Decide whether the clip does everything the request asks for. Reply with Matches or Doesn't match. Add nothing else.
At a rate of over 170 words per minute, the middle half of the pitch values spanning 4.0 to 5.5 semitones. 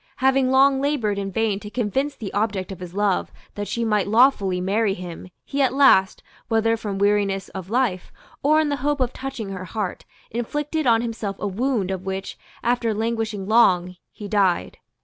Matches